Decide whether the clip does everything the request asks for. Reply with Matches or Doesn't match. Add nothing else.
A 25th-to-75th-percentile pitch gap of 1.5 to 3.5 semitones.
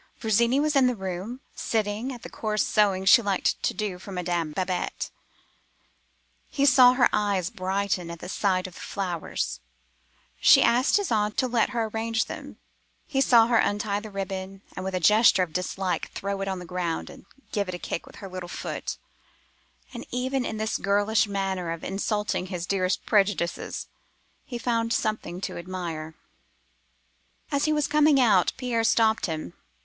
Doesn't match